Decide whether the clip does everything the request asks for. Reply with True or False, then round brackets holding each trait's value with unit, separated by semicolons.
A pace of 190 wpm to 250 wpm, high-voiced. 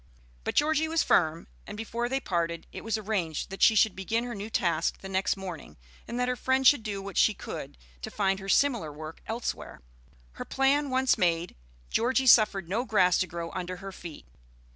True (200 wpm; 200 Hz)